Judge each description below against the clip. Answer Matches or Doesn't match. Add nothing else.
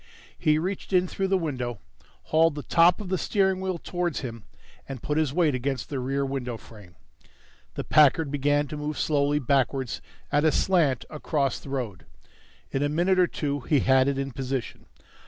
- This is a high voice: Doesn't match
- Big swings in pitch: Doesn't match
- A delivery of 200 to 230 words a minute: Doesn't match